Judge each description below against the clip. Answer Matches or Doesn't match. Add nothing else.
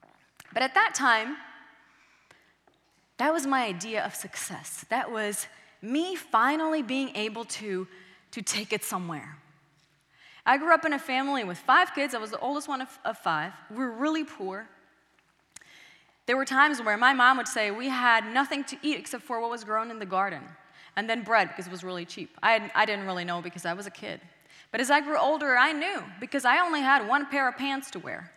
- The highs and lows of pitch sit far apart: Matches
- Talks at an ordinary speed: Doesn't match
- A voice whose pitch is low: Doesn't match